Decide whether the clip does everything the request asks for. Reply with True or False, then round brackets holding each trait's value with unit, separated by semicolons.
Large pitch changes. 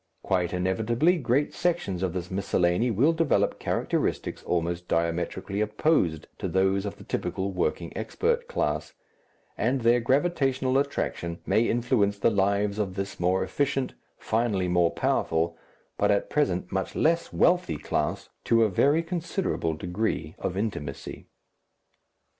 True (6.8 semitones)